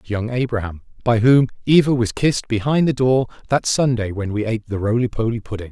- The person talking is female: No, male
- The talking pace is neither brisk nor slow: No, fast, 220 wpm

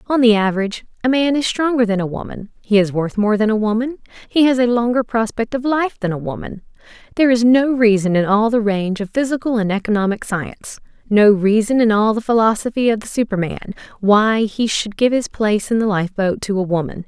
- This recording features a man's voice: No, female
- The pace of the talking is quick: Yes, fast, 220 wpm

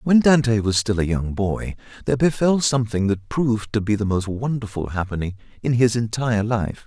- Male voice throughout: Yes, male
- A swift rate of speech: No, average, 190 wpm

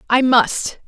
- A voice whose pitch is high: Yes, very high, 250 Hz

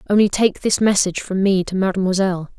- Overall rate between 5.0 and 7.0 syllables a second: Yes, 6.4 syllables/s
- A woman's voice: Yes, female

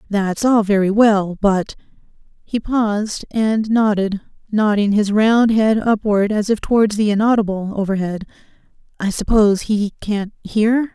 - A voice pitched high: Yes, high, 210 Hz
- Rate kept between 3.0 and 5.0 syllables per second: Yes, 4.4 syllables/s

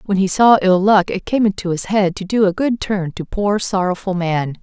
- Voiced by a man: No, female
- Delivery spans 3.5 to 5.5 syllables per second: Yes, 5.0 syllables/s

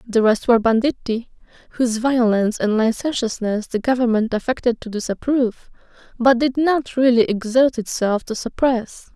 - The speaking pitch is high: Yes, high, 240 Hz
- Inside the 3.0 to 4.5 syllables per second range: No, 5.1 syllables/s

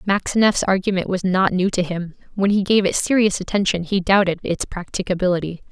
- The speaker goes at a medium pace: Yes, average, 180 wpm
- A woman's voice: Yes, female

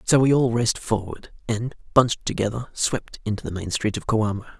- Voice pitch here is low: Yes, low, 115 Hz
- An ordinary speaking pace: Yes, average, 195 wpm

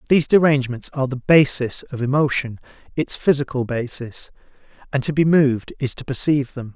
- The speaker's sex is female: No, male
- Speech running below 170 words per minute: Yes, average, 160 wpm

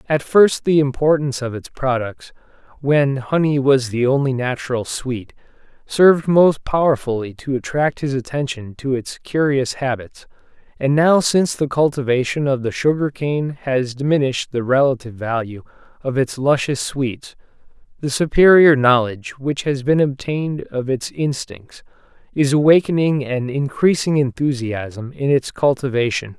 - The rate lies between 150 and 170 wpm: No, average, 140 wpm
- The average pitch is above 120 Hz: Yes, low, 135 Hz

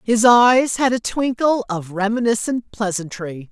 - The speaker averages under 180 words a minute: Yes, slow, 135 wpm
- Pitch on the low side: No, high, 220 Hz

